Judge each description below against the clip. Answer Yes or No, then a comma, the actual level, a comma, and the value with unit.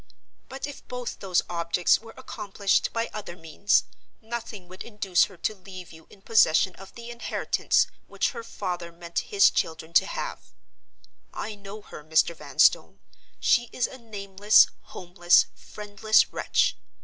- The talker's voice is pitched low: No, high, 200 Hz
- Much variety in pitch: No, average, 4.2 semitones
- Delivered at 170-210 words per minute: No, average, 150 wpm